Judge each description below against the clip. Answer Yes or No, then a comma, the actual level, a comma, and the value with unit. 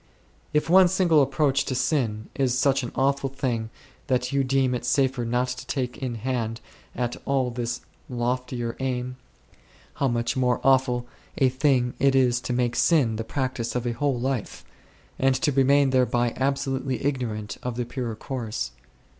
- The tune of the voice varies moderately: No, narrow, 1.9 semitones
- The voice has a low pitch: Yes, low, 130 Hz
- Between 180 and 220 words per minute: No, average, 165 wpm